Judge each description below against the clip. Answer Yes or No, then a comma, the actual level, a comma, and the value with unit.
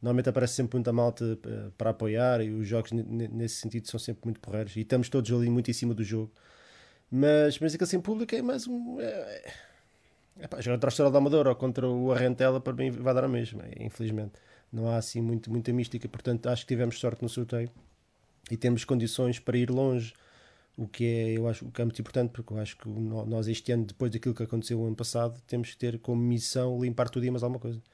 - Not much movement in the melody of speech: Yes, narrow, 1.8 semitones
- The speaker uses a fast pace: Yes, fast, 225 wpm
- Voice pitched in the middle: No, low, 120 Hz